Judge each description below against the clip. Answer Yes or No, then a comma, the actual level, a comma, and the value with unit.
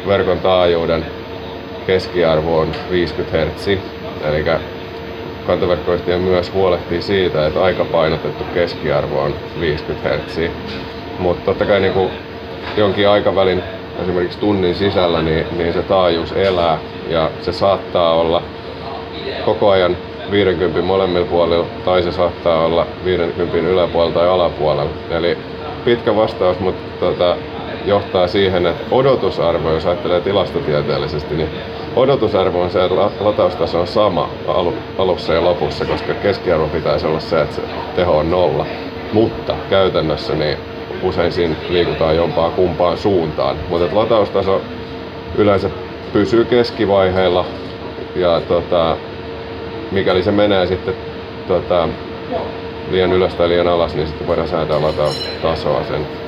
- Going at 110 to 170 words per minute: Yes, average, 120 wpm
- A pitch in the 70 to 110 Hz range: Yes, very low, 90 Hz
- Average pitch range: No, narrow, 1.8 semitones